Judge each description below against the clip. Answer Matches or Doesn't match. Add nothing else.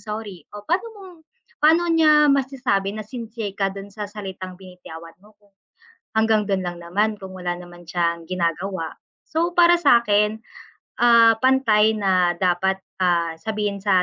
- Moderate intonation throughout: Matches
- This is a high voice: Matches